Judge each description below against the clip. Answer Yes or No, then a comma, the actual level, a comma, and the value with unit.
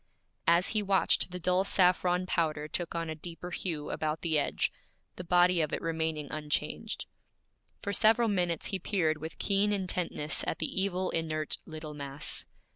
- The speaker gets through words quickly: No, average, 165 wpm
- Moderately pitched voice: Yes, medium, 170 Hz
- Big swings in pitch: No, average, 3.0 semitones